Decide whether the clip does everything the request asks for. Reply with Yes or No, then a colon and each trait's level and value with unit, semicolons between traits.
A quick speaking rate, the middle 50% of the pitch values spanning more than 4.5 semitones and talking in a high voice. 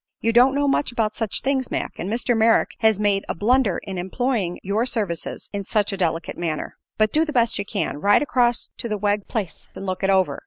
No: fast, 230 wpm; average, 3.8 semitones; high, 215 Hz